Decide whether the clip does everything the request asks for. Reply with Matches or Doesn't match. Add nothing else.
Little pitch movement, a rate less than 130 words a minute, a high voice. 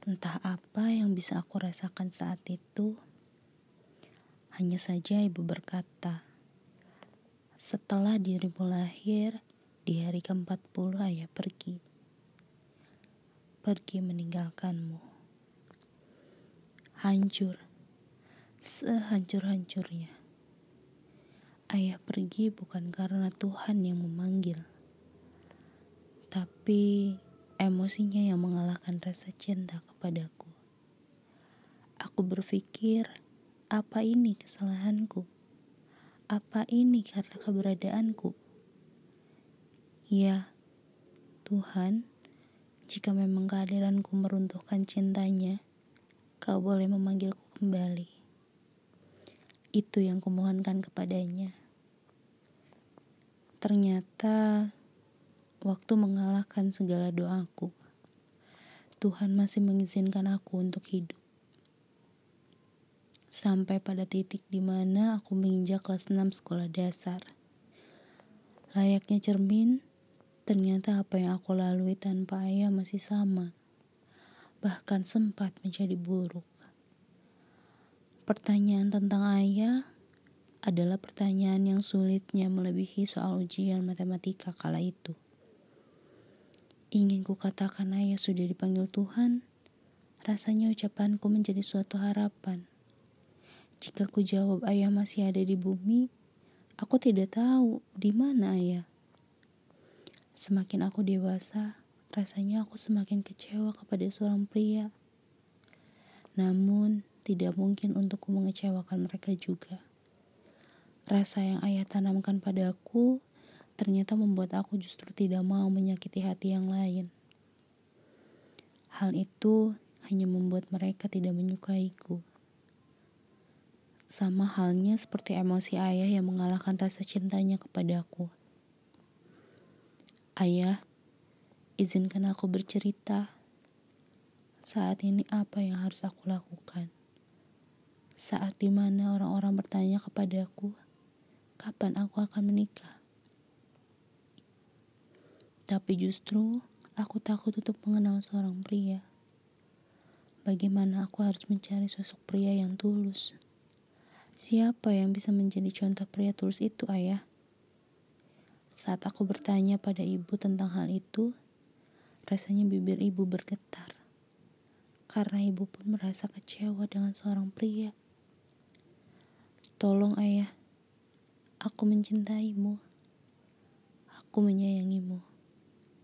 Matches